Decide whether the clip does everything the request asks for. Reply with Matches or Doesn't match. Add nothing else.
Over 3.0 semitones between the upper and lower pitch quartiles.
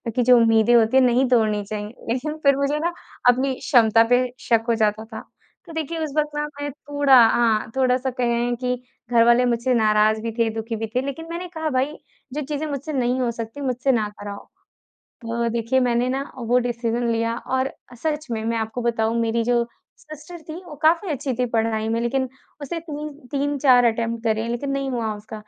Matches